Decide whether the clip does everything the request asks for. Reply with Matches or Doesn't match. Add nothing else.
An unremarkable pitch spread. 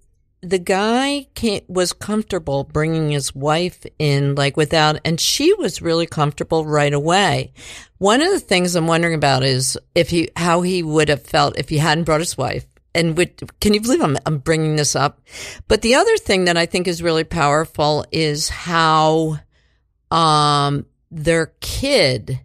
Matches